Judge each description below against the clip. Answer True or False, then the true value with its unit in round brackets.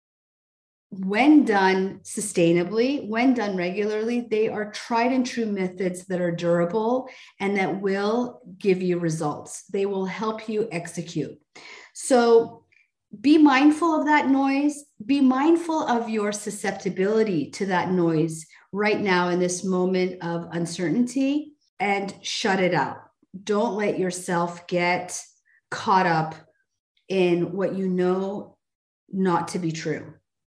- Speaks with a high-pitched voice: True (195 Hz)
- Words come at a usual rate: False (130 wpm)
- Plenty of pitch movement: False (4.6 semitones)